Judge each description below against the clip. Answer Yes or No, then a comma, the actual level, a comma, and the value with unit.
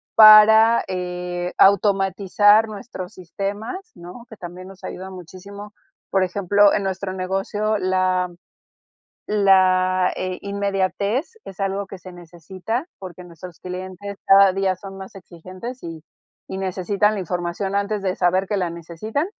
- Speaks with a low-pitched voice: No, high, 190 Hz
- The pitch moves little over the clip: Yes, narrow, 1.8 semitones